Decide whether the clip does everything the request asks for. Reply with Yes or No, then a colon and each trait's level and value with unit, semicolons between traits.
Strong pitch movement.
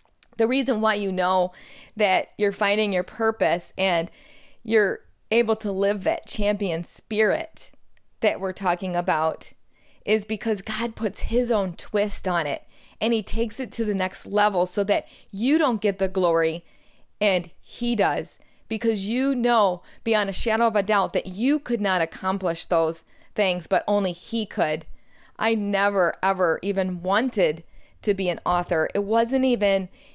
No: average, 3.4 semitones